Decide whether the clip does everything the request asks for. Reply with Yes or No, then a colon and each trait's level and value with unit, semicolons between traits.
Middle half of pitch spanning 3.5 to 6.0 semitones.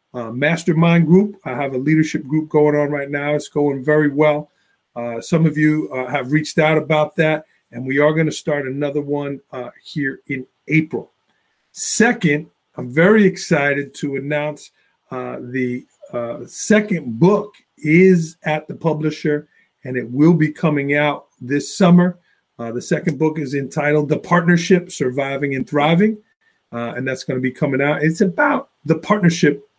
No: average, 2.9 semitones